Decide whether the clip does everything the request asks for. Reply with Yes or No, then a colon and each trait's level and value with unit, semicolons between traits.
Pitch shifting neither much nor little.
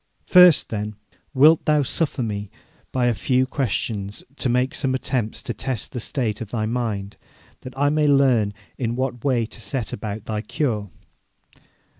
Yes: average, 4.0 semitones